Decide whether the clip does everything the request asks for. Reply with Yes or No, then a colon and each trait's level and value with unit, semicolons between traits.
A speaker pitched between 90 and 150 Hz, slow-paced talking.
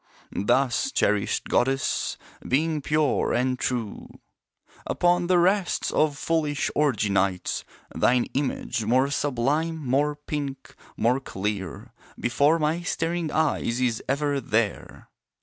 Yes: medium, 140 Hz; slow, 115 wpm